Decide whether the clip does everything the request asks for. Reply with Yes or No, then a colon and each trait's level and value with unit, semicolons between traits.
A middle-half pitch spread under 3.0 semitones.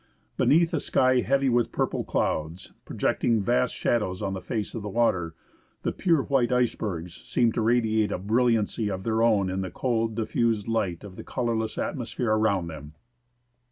No: average, 3.9 semitones